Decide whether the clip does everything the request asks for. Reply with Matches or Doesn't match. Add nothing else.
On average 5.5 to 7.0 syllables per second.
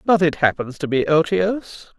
Doesn't match